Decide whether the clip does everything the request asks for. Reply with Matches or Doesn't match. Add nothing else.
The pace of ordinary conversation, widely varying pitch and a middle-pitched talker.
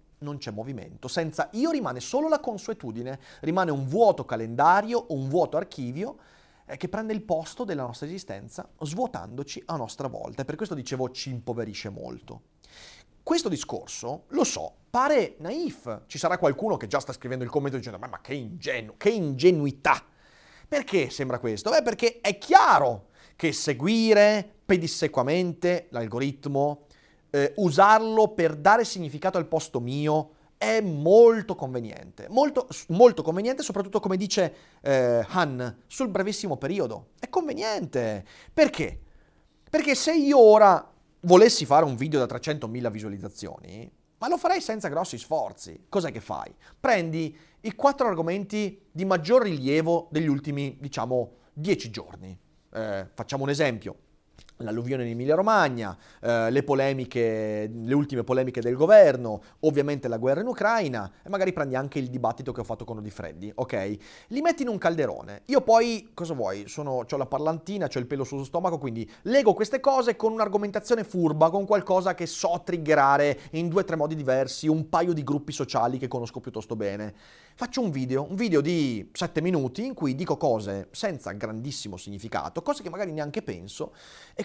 Matches